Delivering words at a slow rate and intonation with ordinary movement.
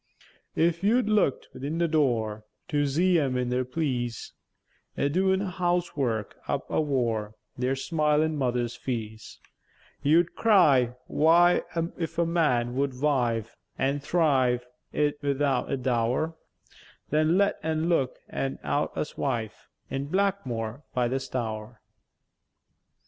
Yes: slow, 125 wpm; average, 4.9 semitones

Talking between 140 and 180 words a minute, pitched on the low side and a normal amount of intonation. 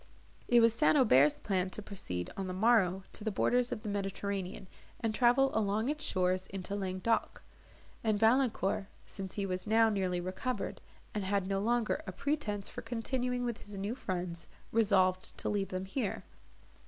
No: average, 170 wpm; high, 205 Hz; average, 3.6 semitones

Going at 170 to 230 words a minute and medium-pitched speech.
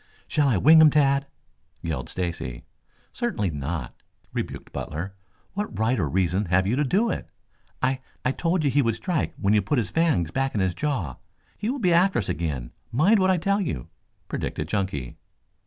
No: average, 190 wpm; low, 120 Hz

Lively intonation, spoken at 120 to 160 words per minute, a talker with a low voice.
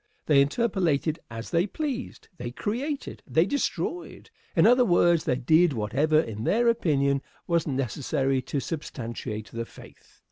No: wide, 6.8 semitones; average, 140 wpm; medium, 155 Hz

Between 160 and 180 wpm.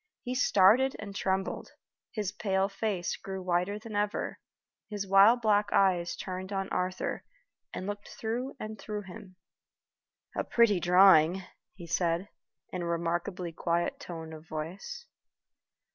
No: slow, 135 wpm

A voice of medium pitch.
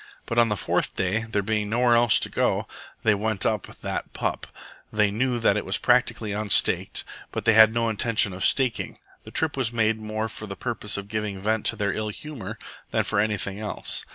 No: low, 110 Hz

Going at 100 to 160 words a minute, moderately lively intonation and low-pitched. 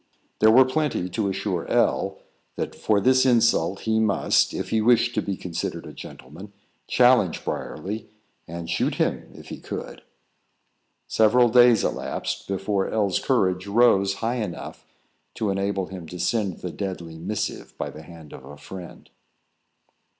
Yes: average, 155 wpm; average, 3.9 semitones; low, 100 Hz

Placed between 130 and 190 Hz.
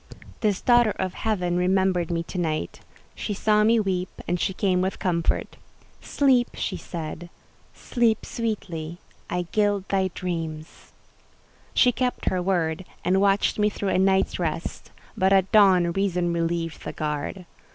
Yes: medium, 185 Hz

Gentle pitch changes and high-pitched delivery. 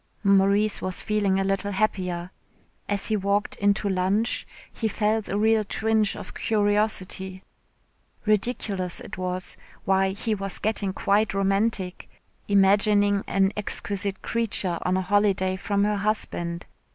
Yes: narrow, 1.8 semitones; high, 200 Hz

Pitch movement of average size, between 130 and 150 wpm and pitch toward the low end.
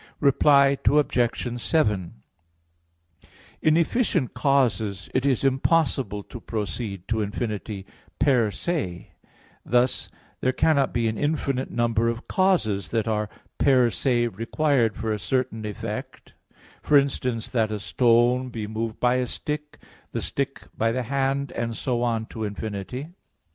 Yes: average, 3.8 semitones; slow, 135 wpm; low, 120 Hz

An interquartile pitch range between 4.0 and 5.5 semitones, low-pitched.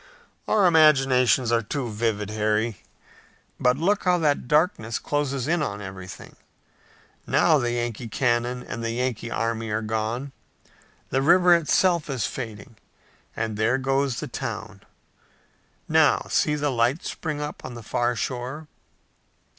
Yes: average, 4.6 semitones; low, 125 Hz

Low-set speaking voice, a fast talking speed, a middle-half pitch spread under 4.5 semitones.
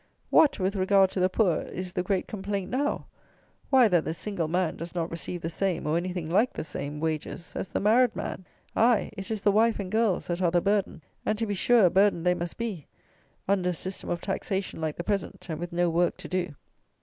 No: medium, 185 Hz; fast, 230 wpm; average, 3.0 semitones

